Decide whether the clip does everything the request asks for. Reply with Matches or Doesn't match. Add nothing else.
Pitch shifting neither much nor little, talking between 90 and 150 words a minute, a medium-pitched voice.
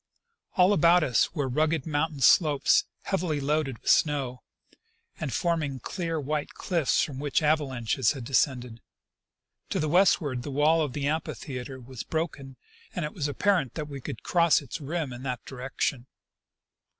Doesn't match